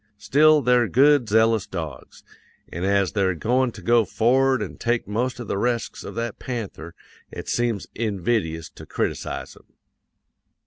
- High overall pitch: No, low, 115 Hz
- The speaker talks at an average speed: Yes, average, 150 wpm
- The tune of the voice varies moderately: Yes, average, 3.8 semitones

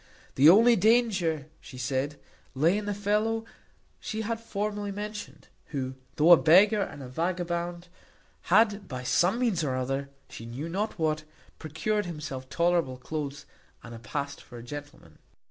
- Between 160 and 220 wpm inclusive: No, average, 150 wpm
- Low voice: No, medium, 170 Hz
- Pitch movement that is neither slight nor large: No, wide, 6.8 semitones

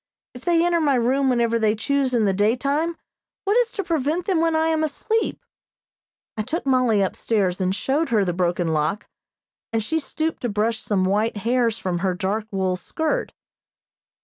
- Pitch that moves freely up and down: Yes, wide, 7.7 semitones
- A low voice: No, high, 235 Hz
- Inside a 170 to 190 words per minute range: Yes, average, 180 wpm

